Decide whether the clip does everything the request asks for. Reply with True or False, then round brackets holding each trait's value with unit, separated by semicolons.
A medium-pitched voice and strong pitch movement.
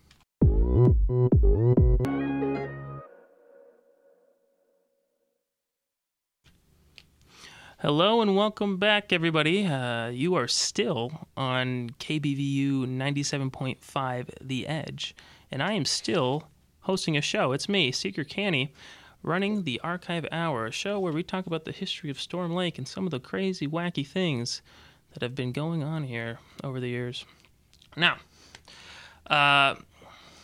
True (150 Hz; 6.8 semitones)